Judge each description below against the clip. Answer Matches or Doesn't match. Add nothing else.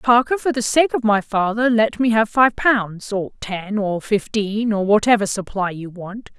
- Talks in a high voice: Matches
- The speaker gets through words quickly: Doesn't match